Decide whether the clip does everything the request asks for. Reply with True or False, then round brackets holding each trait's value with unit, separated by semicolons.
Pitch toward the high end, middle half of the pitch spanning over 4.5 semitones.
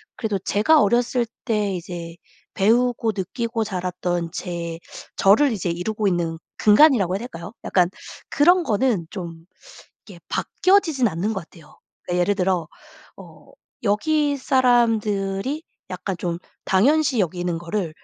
True (200 Hz; 5.4 semitones)